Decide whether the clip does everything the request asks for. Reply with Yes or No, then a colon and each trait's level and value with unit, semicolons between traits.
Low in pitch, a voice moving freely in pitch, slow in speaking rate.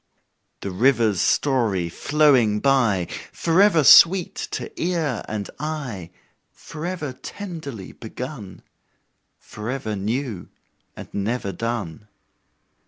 Yes: low, 125 Hz; wide, 6.5 semitones; slow, 90 wpm